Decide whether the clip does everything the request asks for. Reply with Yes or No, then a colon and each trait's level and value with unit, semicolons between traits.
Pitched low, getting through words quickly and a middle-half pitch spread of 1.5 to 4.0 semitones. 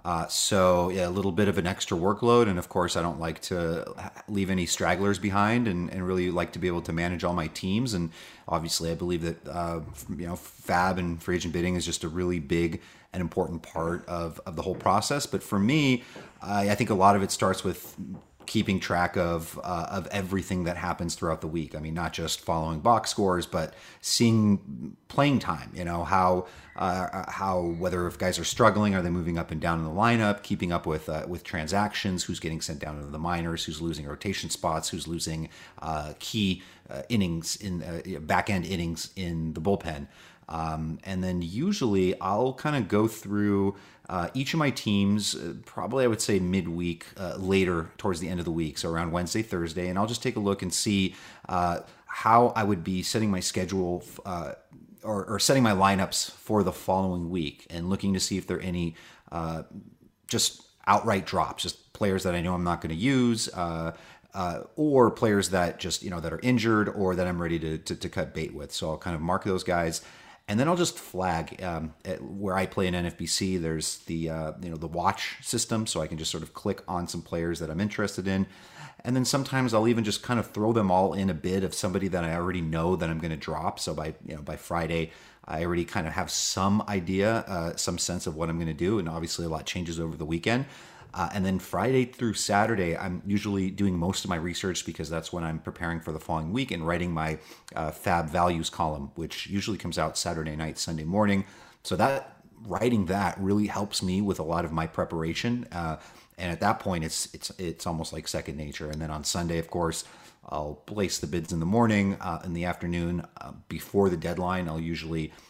Yes: very low, 90 Hz; fast, 220 wpm; average, 3.2 semitones